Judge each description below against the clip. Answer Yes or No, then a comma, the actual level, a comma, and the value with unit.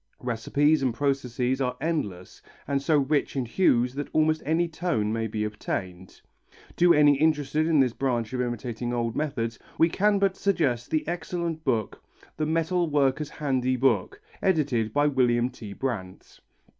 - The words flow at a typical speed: Yes, average, 155 wpm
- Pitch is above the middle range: No, low, 135 Hz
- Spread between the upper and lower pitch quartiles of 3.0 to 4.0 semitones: No, average, 4.8 semitones